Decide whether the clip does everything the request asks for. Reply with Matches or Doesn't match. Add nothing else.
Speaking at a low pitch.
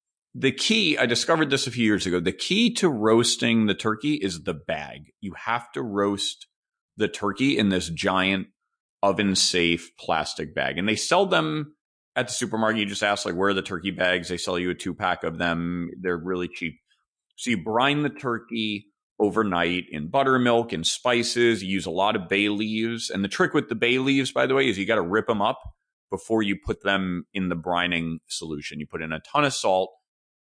Matches